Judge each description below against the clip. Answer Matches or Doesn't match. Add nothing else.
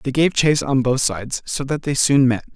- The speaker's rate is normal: Doesn't match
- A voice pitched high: Doesn't match